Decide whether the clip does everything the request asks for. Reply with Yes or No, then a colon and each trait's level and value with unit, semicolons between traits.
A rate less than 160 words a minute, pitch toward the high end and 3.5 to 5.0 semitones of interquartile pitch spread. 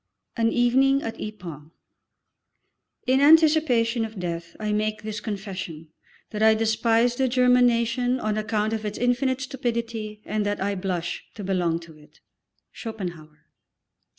Yes: average, 150 wpm; high, 220 Hz; average, 3.8 semitones